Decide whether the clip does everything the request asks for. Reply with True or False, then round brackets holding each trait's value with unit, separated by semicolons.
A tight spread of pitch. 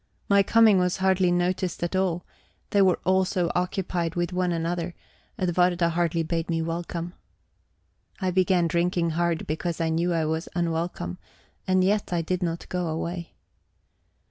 True (1.7 semitones)